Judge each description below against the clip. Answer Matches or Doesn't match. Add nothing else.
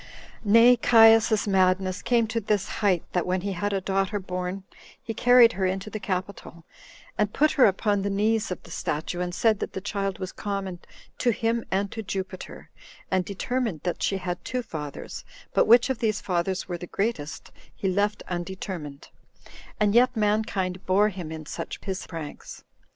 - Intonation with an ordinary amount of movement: Matches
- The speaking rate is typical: Matches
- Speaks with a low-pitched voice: Doesn't match